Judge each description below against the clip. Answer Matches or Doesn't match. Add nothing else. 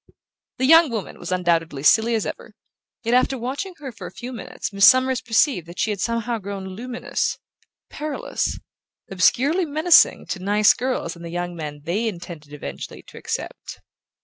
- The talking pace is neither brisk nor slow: Matches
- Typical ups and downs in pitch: Doesn't match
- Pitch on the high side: Matches